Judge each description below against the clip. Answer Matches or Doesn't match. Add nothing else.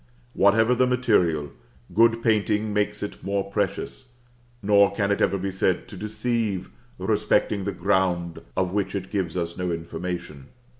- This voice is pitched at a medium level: Doesn't match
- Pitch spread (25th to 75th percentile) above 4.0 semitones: Doesn't match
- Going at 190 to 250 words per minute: Doesn't match